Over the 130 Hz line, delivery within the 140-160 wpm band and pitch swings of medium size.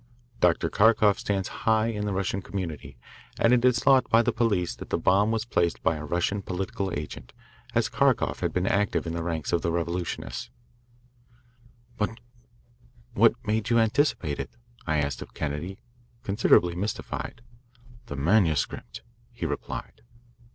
No: very low, 95 Hz; average, 150 wpm; average, 4.7 semitones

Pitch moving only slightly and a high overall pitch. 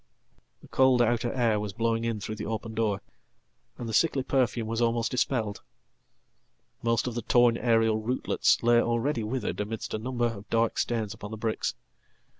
No: narrow, 1.6 semitones; low, 115 Hz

